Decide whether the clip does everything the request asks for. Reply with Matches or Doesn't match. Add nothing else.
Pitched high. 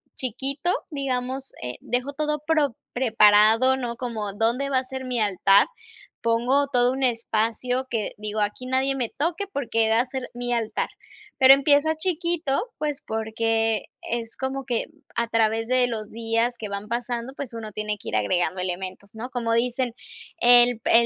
Matches